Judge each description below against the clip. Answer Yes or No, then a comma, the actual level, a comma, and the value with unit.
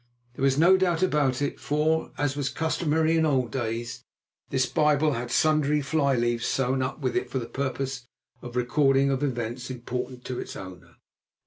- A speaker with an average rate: Yes, average, 185 wpm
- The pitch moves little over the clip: No, average, 3.4 semitones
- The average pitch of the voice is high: No, low, 135 Hz